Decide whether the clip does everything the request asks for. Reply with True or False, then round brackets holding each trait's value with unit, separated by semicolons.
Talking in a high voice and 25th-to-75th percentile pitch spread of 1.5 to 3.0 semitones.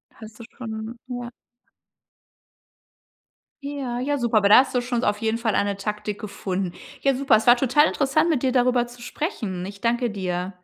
False (235 Hz; 3.4 semitones)